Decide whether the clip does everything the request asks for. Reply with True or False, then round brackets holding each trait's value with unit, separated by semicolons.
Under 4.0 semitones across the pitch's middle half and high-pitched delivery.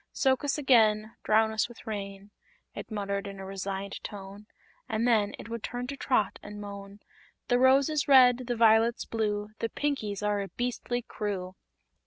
True (3.3 semitones; 215 Hz)